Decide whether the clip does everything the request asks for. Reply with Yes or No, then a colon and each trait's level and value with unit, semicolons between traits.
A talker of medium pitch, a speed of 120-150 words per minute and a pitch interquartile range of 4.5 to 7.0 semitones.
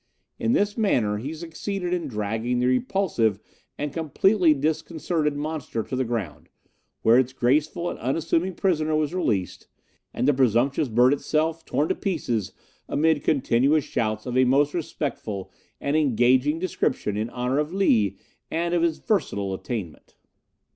Yes: medium, 145 Hz; average, 145 wpm; average, 5.2 semitones